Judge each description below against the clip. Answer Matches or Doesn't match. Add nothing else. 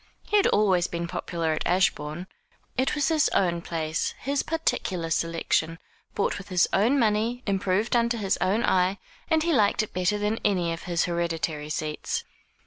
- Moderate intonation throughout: Matches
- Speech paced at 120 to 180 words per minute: Matches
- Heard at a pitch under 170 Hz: Doesn't match